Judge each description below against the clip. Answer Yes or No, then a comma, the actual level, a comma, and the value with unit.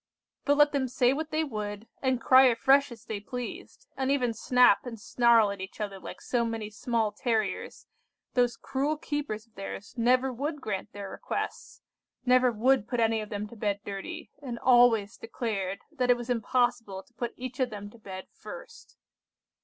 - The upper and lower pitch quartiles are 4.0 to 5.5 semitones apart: No, average, 3.5 semitones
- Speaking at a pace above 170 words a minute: Yes, average, 185 wpm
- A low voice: No, high, 235 Hz